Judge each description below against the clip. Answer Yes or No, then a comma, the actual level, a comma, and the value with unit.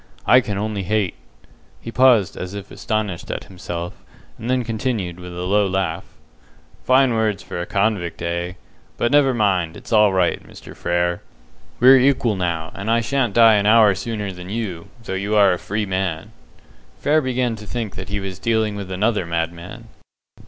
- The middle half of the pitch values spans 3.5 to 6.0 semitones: Yes, average, 4.0 semitones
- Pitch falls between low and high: No, low, 100 Hz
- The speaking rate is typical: Yes, average, 180 wpm